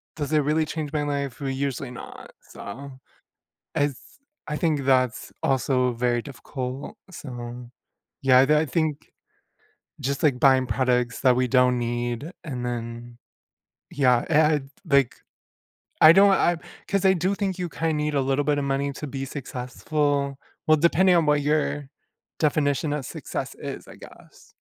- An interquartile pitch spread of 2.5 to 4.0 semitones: Yes, average, 3.0 semitones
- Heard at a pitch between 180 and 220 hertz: No, medium, 140 Hz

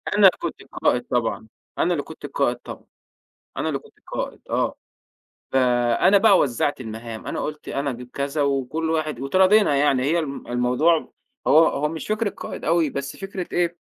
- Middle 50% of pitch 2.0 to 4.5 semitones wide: No, average, 5.1 semitones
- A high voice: No, medium, 145 Hz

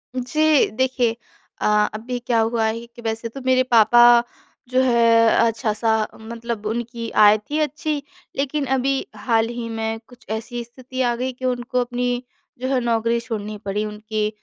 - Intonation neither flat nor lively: No, narrow, 2.3 semitones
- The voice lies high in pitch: Yes, high, 235 Hz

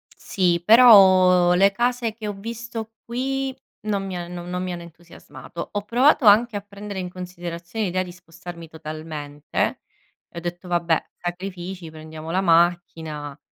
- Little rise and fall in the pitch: No, average, 3.4 semitones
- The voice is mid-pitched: Yes, medium, 180 Hz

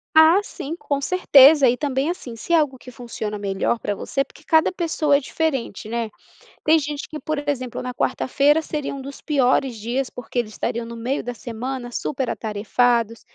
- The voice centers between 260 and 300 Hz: Yes, very high, 265 Hz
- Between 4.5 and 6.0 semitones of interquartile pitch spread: No, average, 4.0 semitones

